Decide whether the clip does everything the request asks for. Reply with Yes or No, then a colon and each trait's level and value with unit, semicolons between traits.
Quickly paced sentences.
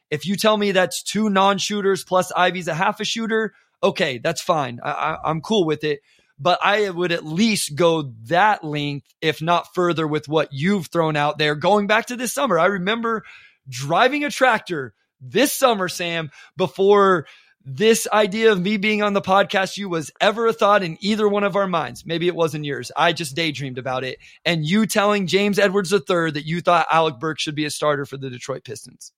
Yes: fast, 210 wpm